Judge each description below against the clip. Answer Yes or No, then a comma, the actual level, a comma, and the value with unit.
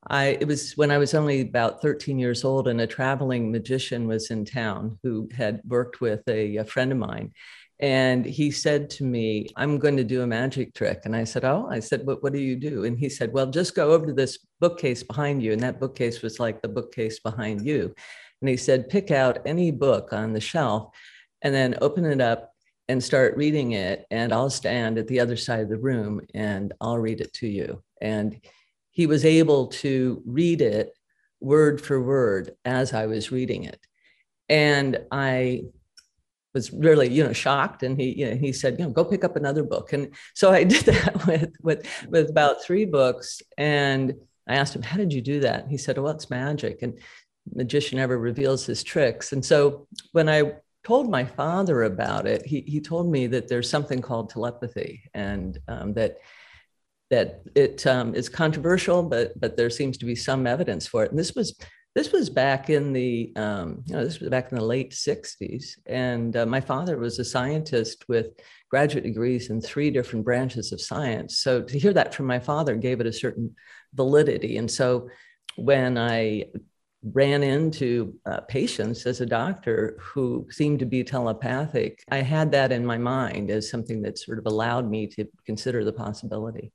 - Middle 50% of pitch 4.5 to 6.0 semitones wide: No, average, 4.1 semitones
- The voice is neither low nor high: No, low, 130 Hz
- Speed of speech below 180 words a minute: No, average, 200 wpm